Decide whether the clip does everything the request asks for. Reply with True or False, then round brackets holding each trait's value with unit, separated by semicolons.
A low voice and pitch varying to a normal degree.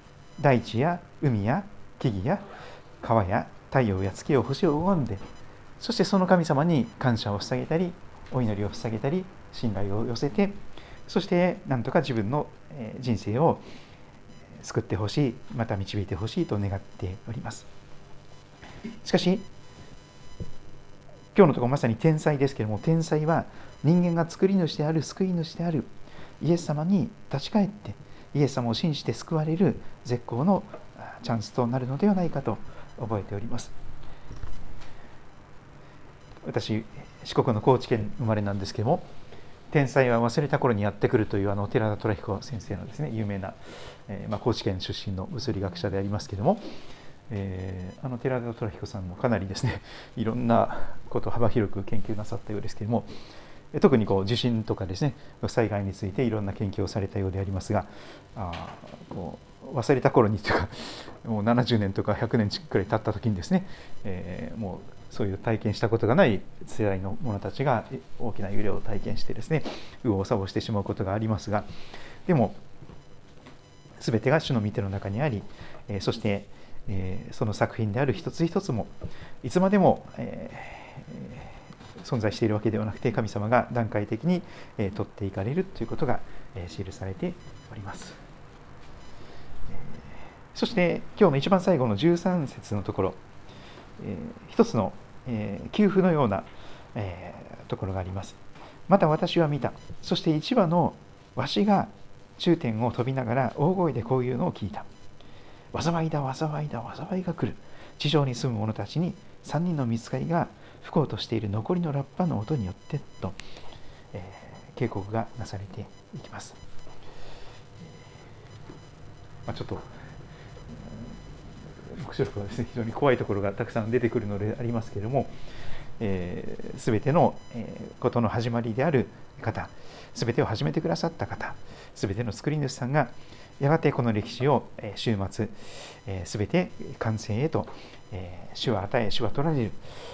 False (120 Hz; 5.7 semitones)